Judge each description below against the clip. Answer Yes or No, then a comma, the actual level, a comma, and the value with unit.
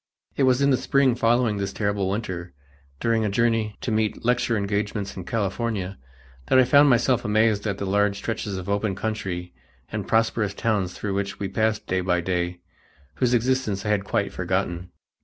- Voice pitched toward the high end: No, low, 105 Hz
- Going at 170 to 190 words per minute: Yes, average, 180 wpm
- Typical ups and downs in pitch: Yes, average, 3.0 semitones